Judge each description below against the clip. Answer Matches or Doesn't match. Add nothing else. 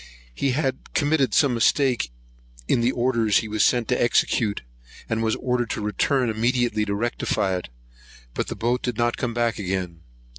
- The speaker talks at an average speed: Matches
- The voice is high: Doesn't match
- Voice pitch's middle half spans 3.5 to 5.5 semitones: Doesn't match